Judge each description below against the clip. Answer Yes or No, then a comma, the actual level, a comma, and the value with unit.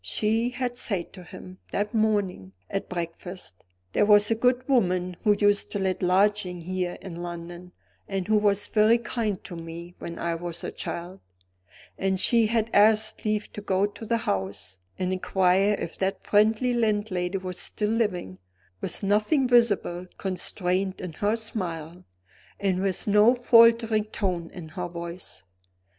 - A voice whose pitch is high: Yes, high, 195 Hz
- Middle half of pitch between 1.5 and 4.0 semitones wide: Yes, average, 3.4 semitones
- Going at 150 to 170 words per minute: Yes, average, 155 wpm